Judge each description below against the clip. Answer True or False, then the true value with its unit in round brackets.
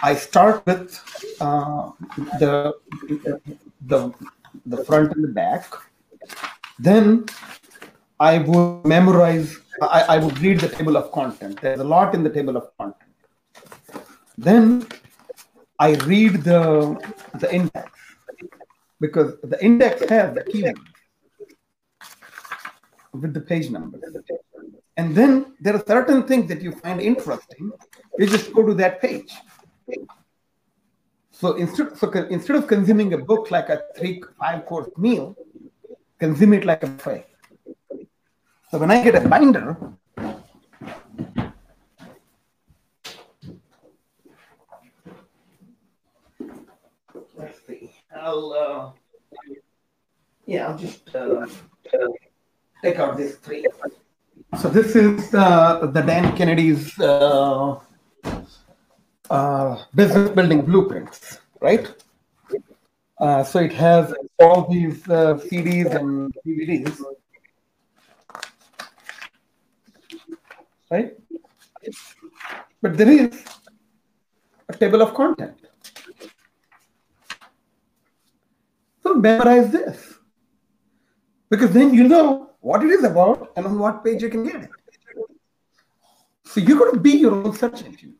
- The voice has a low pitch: False (200 Hz)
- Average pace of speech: False (110 wpm)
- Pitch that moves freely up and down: True (7.1 semitones)